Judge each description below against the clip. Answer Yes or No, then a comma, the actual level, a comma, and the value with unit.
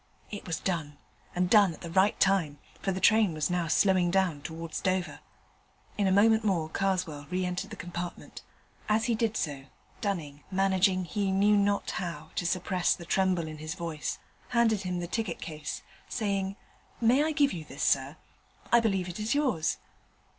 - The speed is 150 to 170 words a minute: No, average, 180 wpm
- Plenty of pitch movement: No, average, 3.4 semitones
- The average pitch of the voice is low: No, medium, 185 Hz